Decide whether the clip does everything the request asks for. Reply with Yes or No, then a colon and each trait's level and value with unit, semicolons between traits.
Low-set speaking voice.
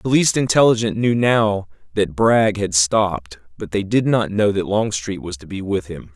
Yes: low, 100 Hz